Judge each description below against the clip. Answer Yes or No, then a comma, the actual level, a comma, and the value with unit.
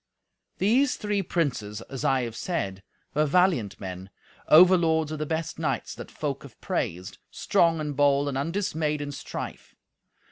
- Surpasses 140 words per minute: Yes, average, 150 wpm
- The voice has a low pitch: No, medium, 150 Hz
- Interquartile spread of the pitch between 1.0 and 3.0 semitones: No, average, 4.2 semitones